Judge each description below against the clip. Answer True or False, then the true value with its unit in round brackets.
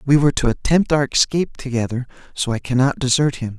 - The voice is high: False (130 Hz)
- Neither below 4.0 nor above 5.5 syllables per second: False (6.3 syllables/s)